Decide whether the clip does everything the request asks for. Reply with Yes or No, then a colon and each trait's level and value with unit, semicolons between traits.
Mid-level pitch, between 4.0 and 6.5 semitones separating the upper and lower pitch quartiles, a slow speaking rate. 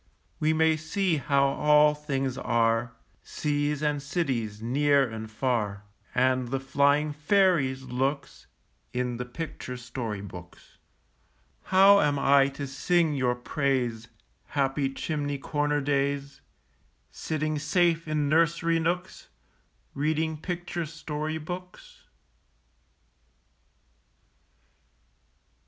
No: medium, 145 Hz; average, 3.3 semitones; slow, 100 wpm